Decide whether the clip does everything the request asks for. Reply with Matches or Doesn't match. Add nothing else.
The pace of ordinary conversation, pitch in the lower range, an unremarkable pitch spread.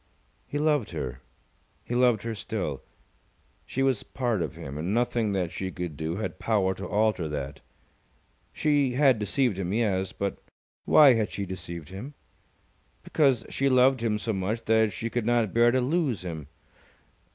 Matches